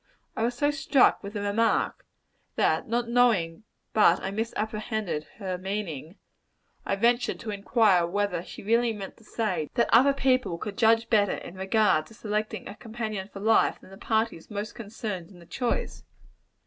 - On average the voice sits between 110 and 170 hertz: No, high, 215 Hz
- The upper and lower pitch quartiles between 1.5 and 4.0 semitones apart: Yes, average, 3.1 semitones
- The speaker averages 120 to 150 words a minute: No, average, 170 wpm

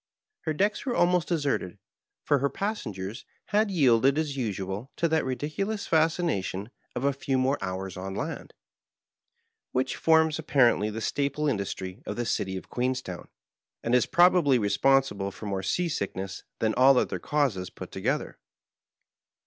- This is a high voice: No, low, 130 Hz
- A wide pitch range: Yes, wide, 7.6 semitones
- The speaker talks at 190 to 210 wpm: No, average, 150 wpm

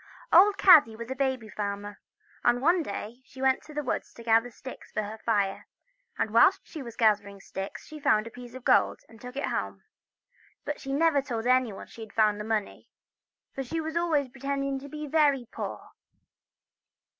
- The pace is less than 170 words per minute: No, average, 195 wpm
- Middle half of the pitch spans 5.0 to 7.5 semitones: No, average, 4.3 semitones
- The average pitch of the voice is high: Yes, very high, 250 Hz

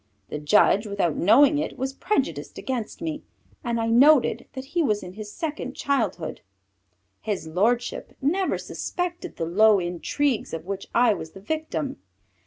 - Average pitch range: No, wide, 6.9 semitones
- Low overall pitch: No, high, 230 Hz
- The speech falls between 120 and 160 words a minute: Yes, average, 155 wpm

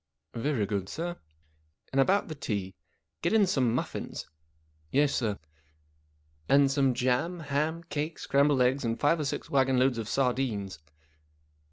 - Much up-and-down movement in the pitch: Yes, wide, 6.2 semitones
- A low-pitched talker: Yes, low, 130 Hz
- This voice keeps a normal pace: Yes, average, 165 wpm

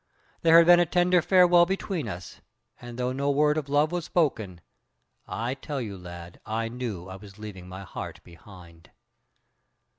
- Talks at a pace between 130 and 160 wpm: No, average, 170 wpm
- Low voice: Yes, low, 125 Hz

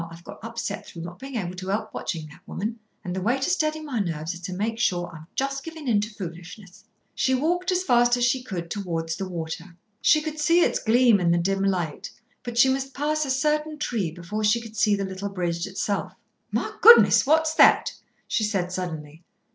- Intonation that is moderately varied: No, wide, 7.0 semitones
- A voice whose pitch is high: Yes, high, 210 Hz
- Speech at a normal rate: No, fast, 215 wpm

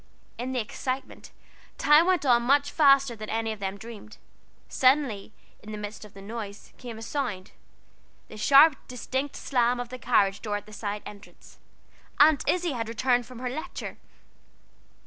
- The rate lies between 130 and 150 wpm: No, average, 165 wpm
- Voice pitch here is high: Yes, high, 240 Hz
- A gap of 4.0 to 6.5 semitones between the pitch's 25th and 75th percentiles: Yes, average, 4.3 semitones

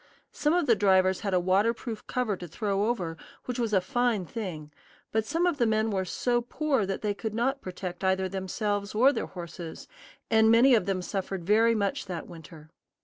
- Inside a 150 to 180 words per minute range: No, average, 200 wpm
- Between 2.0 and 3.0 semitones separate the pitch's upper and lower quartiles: No, average, 3.8 semitones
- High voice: Yes, high, 205 Hz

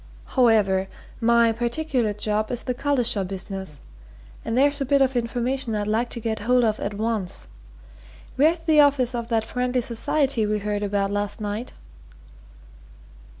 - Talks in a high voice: Yes, high, 230 Hz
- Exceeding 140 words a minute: Yes, average, 150 wpm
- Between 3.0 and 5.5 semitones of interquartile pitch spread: Yes, average, 3.4 semitones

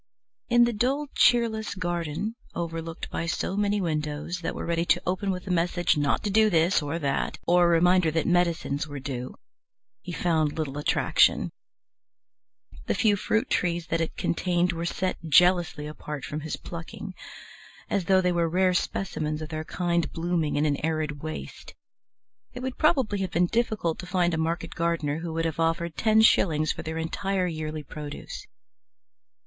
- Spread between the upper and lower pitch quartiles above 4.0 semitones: No, average, 2.9 semitones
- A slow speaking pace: No, average, 175 wpm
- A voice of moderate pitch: Yes, medium, 170 Hz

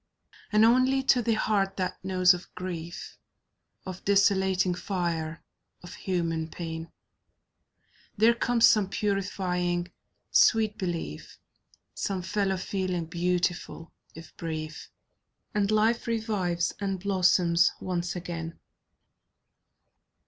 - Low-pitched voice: No, medium, 185 Hz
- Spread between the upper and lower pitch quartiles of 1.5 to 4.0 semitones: Yes, average, 2.8 semitones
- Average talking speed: No, slow, 100 wpm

